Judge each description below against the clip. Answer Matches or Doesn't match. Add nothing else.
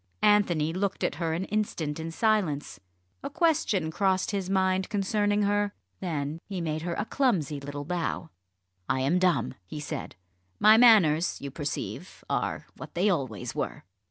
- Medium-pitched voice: Matches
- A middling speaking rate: Matches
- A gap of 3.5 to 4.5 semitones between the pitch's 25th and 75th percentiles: Doesn't match